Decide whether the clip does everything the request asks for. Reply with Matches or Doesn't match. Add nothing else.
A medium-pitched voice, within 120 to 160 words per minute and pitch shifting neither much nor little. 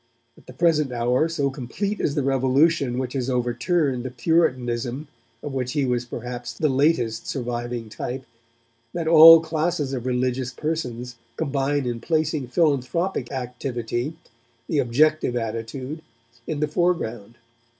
Doesn't match